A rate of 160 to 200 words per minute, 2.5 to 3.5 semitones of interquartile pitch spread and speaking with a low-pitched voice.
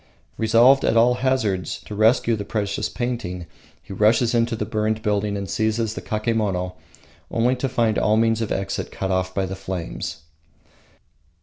Yes: average, 165 wpm; average, 2.8 semitones; low, 110 Hz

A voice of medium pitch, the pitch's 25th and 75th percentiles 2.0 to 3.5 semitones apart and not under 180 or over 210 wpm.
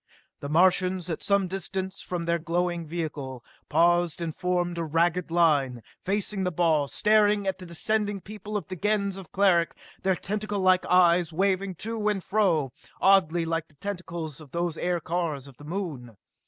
No: medium, 175 Hz; average, 2.9 semitones; average, 165 wpm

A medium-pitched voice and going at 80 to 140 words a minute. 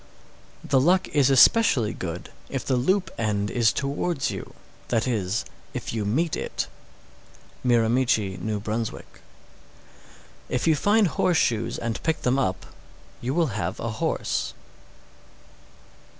No: low, 125 Hz; slow, 135 wpm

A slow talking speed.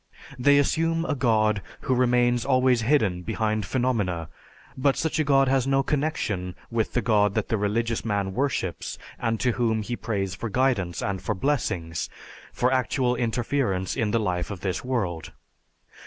No: average, 165 wpm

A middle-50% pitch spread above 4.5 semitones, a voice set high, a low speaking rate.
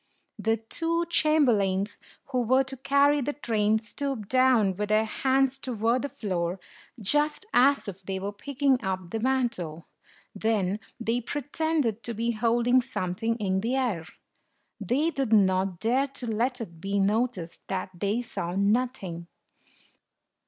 No: average, 5.0 semitones; high, 230 Hz; average, 145 wpm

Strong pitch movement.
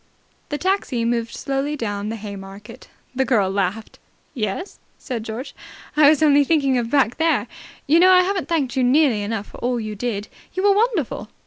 Yes: wide, 5.8 semitones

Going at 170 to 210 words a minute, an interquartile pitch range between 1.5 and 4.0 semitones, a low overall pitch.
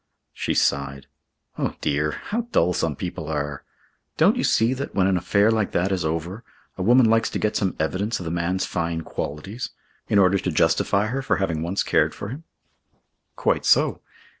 No: average, 190 wpm; average, 4.7 semitones; very low, 95 Hz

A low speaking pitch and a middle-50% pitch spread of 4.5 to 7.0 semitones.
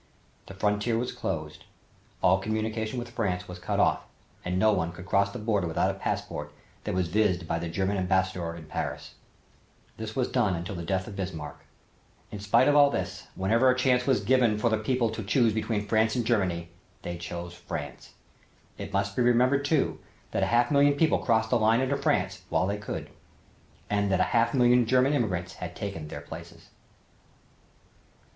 Yes: low, 105 Hz; average, 4.8 semitones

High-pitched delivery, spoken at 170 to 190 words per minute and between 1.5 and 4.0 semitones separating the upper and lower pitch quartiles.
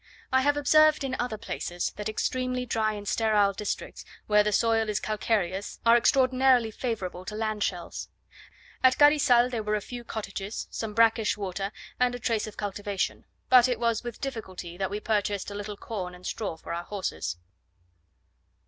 Yes: high, 215 Hz; average, 175 wpm; average, 3.3 semitones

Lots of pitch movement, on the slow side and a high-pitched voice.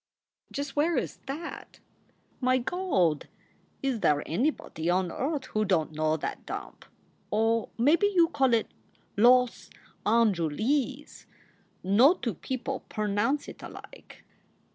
Yes: wide, 6.3 semitones; slow, 120 wpm; high, 240 Hz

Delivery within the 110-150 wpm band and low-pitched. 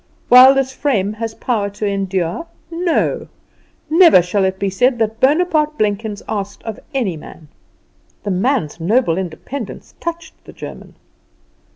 No: average, 140 wpm; high, 220 Hz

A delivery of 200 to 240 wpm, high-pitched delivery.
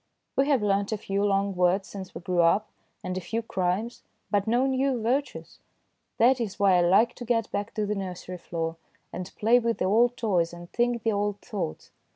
Yes: fast, 205 wpm; high, 205 Hz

